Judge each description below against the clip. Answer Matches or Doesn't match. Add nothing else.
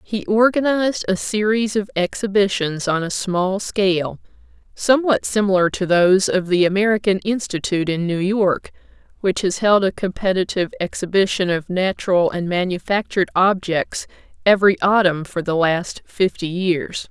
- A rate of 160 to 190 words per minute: Doesn't match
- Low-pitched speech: Doesn't match